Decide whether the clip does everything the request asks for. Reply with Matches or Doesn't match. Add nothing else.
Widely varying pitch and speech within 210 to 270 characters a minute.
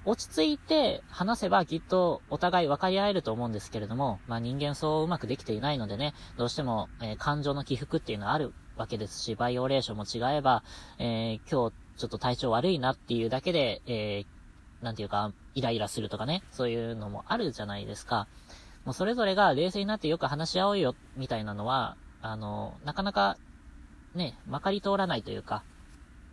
Doesn't match